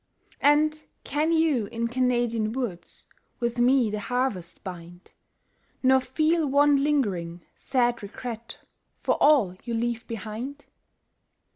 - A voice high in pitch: Yes, high, 240 Hz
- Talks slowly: Yes, slow, 115 wpm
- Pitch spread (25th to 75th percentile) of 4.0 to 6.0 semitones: Yes, average, 4.5 semitones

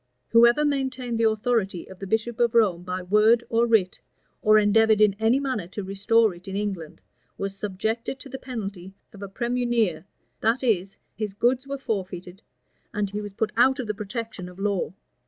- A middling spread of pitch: Yes, average, 3.4 semitones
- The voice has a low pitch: No, high, 215 Hz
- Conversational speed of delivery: Yes, average, 185 wpm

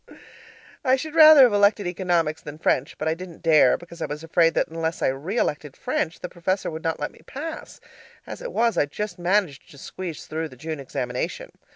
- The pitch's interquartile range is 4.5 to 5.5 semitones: Yes, average, 4.8 semitones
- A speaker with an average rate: No, fast, 210 wpm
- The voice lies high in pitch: No, medium, 165 Hz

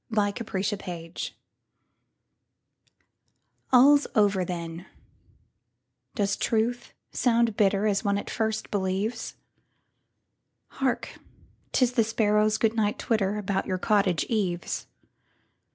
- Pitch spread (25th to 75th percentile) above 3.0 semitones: No, average, 2.7 semitones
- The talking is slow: Yes, slow, 90 wpm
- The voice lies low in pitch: No, high, 210 Hz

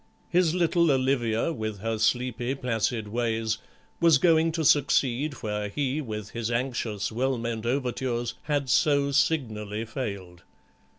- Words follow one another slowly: Yes, slow, 130 wpm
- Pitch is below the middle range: Yes, low, 120 Hz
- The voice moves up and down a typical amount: Yes, average, 4.2 semitones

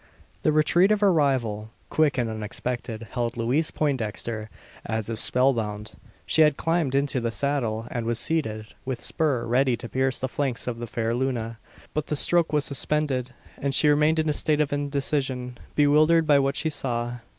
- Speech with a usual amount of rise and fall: Yes, average, 4.2 semitones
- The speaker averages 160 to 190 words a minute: Yes, average, 185 wpm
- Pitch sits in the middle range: No, low, 130 Hz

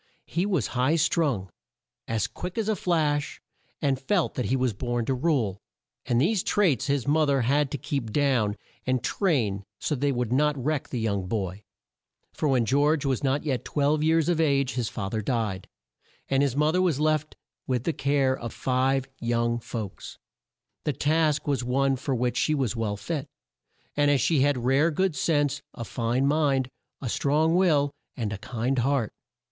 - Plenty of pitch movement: No, average, 3.8 semitones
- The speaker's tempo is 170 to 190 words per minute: Yes, average, 185 wpm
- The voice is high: No, low, 135 Hz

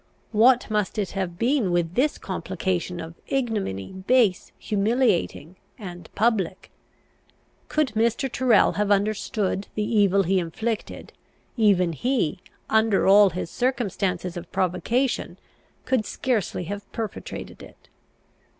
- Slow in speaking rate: Yes, slow, 115 wpm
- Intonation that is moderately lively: Yes, average, 4.2 semitones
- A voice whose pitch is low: No, high, 205 Hz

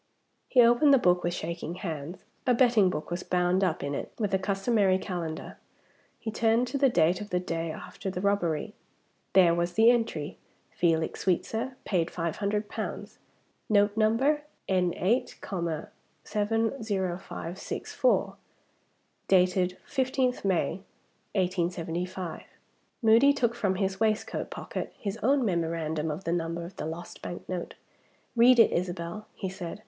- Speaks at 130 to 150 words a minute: Yes, average, 140 wpm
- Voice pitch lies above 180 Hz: Yes, high, 190 Hz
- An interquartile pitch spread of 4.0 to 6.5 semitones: Yes, average, 4.4 semitones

